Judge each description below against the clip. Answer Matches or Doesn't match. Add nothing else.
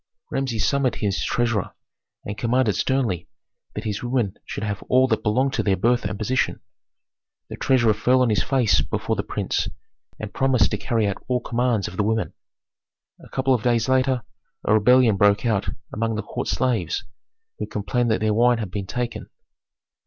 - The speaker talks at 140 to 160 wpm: Doesn't match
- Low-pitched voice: Matches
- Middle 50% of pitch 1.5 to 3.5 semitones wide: Matches